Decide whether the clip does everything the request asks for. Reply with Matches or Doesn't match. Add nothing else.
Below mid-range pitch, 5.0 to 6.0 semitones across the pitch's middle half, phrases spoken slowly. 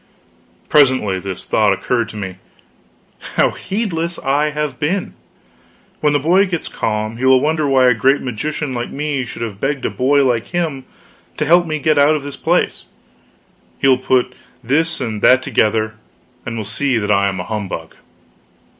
Doesn't match